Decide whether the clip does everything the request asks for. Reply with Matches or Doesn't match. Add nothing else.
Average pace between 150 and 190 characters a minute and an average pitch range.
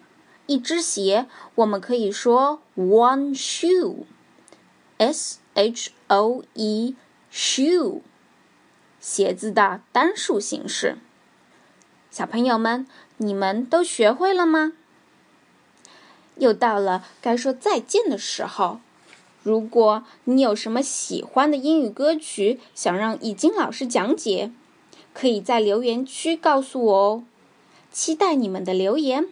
Doesn't match